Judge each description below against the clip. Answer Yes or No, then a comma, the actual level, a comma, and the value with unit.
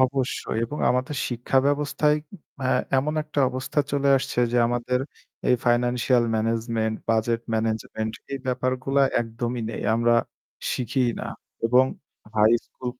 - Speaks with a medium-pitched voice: No, low, 125 Hz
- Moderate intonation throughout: No, narrow, 2.3 semitones